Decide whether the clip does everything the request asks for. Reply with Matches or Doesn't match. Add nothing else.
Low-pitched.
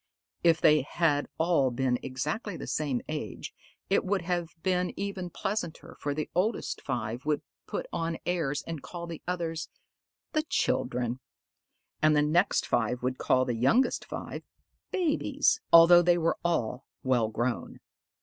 Doesn't match